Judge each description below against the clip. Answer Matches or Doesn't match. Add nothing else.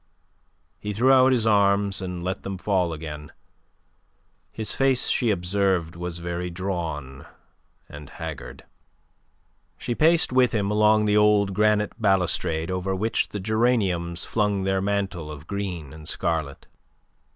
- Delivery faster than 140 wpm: Doesn't match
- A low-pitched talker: Matches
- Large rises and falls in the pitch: Doesn't match